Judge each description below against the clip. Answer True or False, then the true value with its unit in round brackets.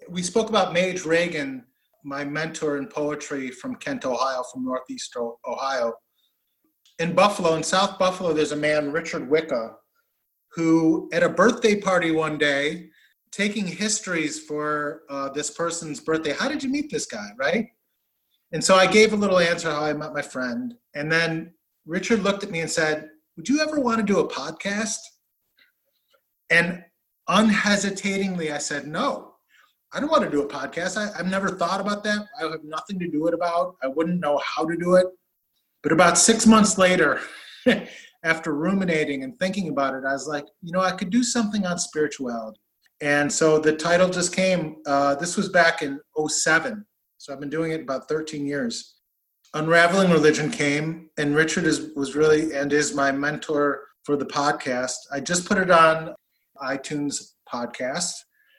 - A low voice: False (165 Hz)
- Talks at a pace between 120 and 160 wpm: False (175 wpm)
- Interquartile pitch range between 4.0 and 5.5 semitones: True (4.7 semitones)